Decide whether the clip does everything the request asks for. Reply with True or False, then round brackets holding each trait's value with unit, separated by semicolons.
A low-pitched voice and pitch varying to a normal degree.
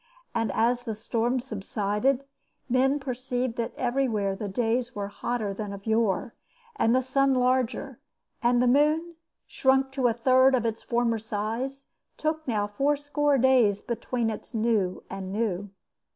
False (240 Hz; 3.3 semitones)